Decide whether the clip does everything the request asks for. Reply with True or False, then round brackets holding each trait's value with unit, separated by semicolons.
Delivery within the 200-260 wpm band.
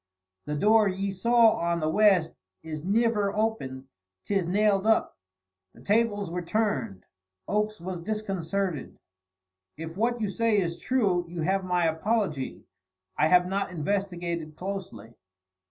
False (135 wpm)